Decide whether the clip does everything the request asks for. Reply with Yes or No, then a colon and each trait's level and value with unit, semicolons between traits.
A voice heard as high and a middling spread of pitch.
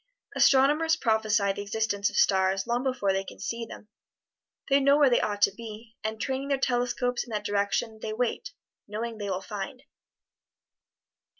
Yes: high, 220 Hz; average, 3.7 semitones